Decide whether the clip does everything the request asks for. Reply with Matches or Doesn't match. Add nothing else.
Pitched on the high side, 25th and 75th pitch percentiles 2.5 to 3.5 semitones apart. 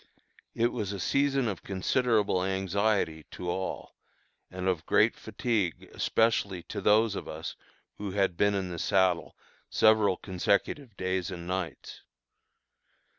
Doesn't match